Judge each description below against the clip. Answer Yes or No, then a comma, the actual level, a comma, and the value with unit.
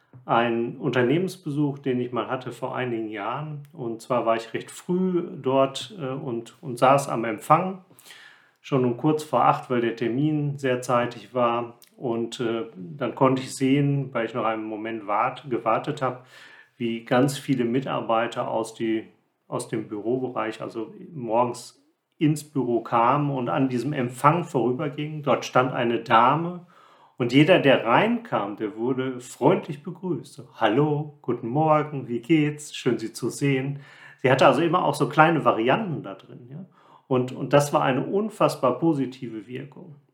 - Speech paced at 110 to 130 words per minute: No, average, 160 wpm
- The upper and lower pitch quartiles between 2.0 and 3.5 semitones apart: No, average, 4.1 semitones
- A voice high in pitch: No, low, 130 Hz